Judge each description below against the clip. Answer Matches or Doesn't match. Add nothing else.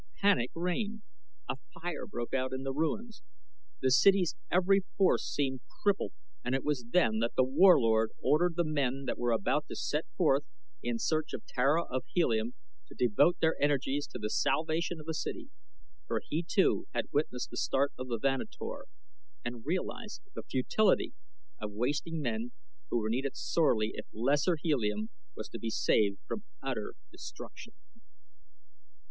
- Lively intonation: Matches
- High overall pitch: Doesn't match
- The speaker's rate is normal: Matches